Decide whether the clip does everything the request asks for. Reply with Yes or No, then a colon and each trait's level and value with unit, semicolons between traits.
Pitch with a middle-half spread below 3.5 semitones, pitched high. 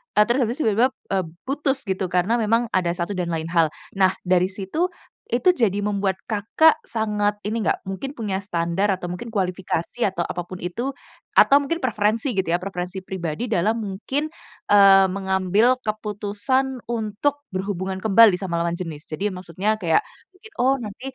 No: average, 4.0 semitones; high, 200 Hz